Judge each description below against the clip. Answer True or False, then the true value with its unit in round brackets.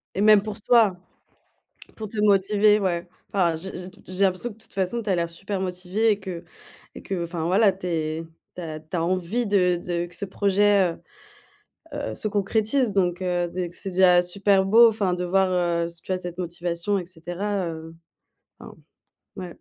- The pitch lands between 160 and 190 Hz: True (185 Hz)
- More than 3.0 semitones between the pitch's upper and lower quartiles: False (2.6 semitones)